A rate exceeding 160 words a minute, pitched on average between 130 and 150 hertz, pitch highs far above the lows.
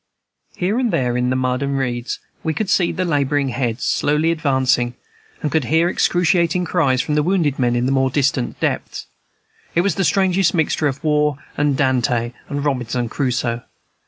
No: average, 175 wpm; medium, 140 Hz; average, 4.5 semitones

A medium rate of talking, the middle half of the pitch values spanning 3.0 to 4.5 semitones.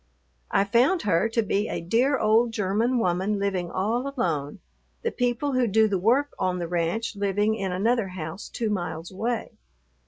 Yes: average, 175 wpm; average, 4.2 semitones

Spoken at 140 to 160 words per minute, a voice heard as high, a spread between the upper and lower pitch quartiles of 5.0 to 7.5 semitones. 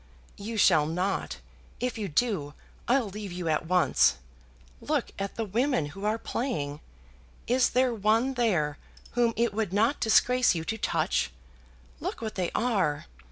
Yes: average, 155 wpm; high, 210 Hz; wide, 5.5 semitones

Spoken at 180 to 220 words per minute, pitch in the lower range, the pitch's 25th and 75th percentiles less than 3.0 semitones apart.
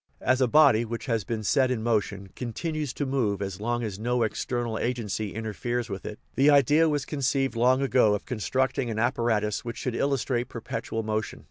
No: average, 190 wpm; low, 120 Hz; average, 3.3 semitones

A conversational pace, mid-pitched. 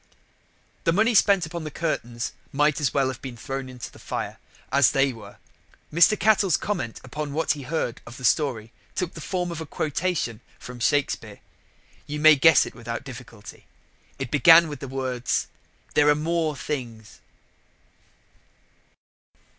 Yes: average, 155 wpm; medium, 145 Hz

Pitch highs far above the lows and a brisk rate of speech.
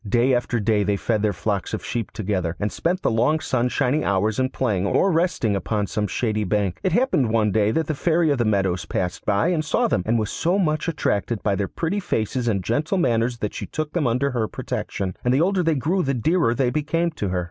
Yes: wide, 6.9 semitones; fast, 235 wpm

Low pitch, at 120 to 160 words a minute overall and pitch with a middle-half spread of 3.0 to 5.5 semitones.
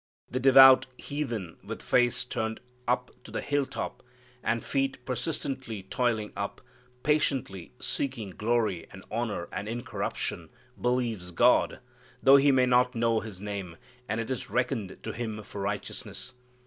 Yes: low, 120 Hz; average, 145 wpm; average, 3.7 semitones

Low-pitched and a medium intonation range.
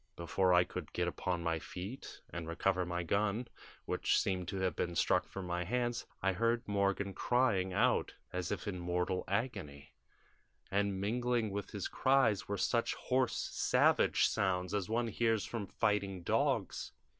Yes: low, 100 Hz; average, 4.0 semitones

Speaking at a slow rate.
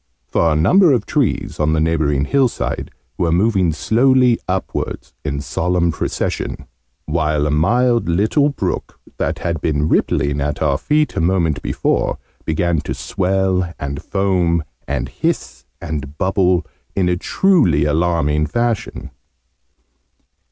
Yes: slow, 130 wpm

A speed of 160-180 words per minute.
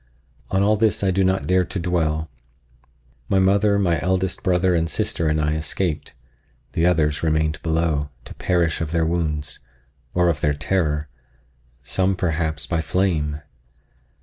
No: average, 150 wpm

